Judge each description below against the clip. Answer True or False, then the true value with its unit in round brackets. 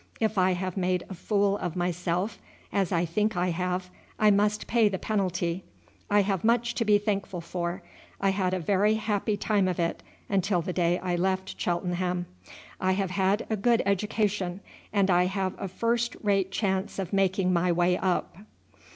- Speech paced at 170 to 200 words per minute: True (180 wpm)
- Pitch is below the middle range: False (190 Hz)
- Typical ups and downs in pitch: False (2.3 semitones)